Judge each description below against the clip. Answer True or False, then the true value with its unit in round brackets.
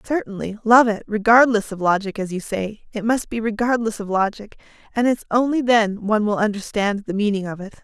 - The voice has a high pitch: True (215 Hz)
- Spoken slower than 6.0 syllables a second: True (5.5 syllables/s)